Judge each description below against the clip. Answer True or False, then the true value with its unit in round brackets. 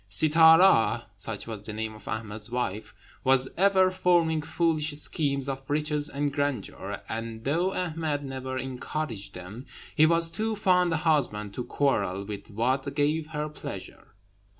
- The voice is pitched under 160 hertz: True (140 Hz)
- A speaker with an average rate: True (150 wpm)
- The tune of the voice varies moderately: False (6.2 semitones)